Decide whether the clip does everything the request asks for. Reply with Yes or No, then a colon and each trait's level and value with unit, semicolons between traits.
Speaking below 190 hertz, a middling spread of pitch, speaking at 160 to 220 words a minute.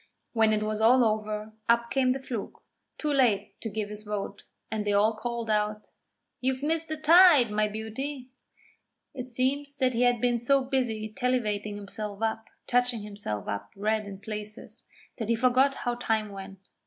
No: high, 225 Hz; average, 3.2 semitones; average, 175 wpm